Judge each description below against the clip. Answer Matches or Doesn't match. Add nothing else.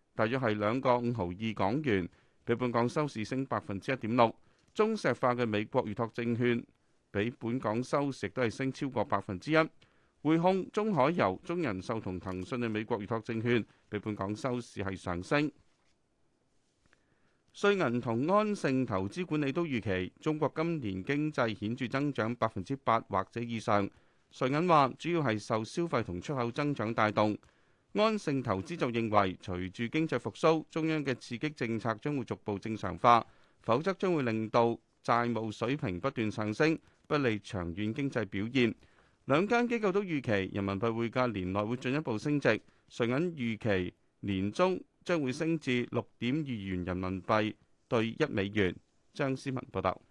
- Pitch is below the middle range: Matches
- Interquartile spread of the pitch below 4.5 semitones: Doesn't match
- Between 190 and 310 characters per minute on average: Matches